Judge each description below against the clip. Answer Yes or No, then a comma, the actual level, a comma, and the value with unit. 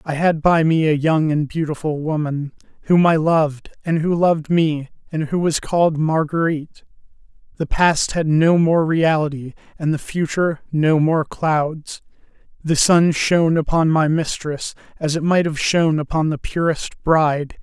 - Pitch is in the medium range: Yes, medium, 155 Hz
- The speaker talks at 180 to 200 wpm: No, average, 165 wpm